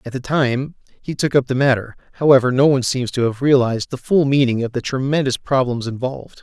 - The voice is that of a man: Yes, male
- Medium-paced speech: No, fast, 215 wpm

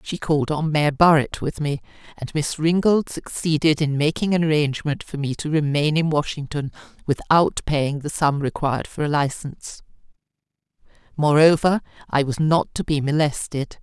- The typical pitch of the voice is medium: Yes, medium, 150 Hz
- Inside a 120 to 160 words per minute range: Yes, average, 155 wpm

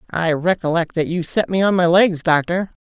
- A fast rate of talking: Yes, fast, 210 wpm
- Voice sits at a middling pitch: Yes, medium, 170 Hz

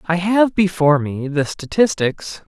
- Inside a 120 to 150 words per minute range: Yes, average, 140 wpm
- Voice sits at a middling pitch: Yes, medium, 170 Hz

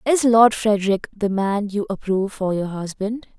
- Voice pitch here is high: Yes, high, 205 Hz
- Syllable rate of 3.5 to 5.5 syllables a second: Yes, 4.8 syllables/s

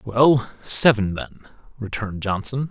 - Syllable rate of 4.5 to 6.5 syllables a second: No, 4.2 syllables/s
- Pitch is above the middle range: No, low, 115 Hz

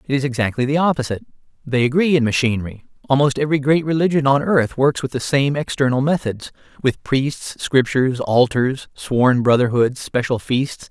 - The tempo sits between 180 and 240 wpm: No, average, 160 wpm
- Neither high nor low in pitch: No, low, 130 Hz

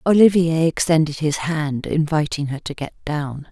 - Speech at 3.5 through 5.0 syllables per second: Yes, 4.6 syllables/s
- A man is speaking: No, female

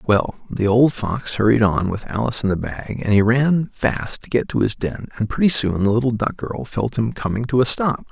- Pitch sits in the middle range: No, low, 115 Hz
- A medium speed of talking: No, fast, 245 wpm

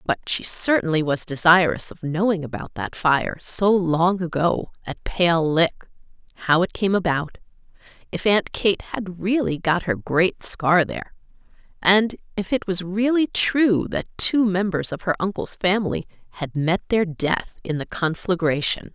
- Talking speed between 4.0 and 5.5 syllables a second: Yes, 4.3 syllables/s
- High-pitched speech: No, medium, 180 Hz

